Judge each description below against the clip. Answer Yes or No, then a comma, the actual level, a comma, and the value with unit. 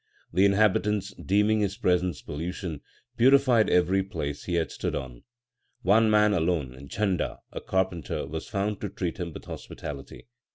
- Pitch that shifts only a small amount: No, average, 3.9 semitones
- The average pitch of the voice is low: Yes, very low, 95 Hz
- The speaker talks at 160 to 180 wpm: No, average, 150 wpm